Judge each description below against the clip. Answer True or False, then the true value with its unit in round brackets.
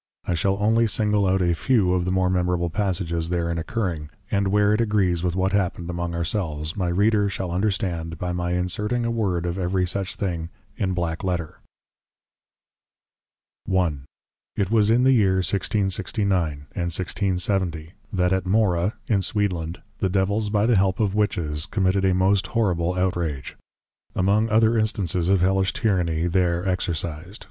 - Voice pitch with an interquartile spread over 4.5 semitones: False (2.8 semitones)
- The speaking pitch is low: True (95 Hz)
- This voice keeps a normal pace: True (160 wpm)